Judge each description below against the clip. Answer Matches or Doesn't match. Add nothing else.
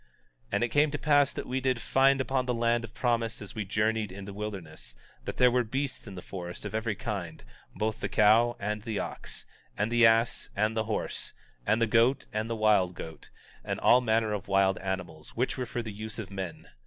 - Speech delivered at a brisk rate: Matches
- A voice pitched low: Matches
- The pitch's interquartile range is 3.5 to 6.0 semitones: Doesn't match